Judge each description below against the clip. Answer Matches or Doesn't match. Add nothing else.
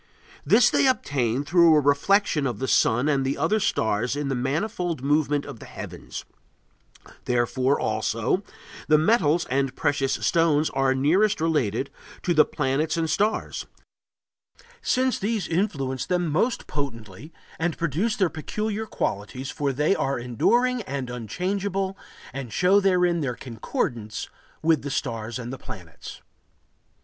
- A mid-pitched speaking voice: Matches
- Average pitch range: Doesn't match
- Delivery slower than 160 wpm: Matches